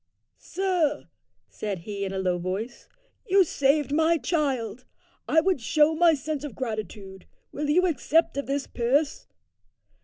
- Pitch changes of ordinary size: No, wide, 6.5 semitones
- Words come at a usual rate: Yes, average, 145 wpm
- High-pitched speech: Yes, very high, 280 Hz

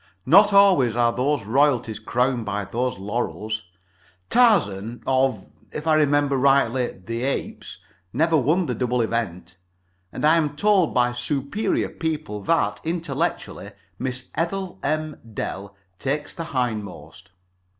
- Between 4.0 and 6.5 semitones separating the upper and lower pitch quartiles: Yes, average, 5.2 semitones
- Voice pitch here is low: Yes, low, 130 Hz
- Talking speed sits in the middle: No, slow, 130 wpm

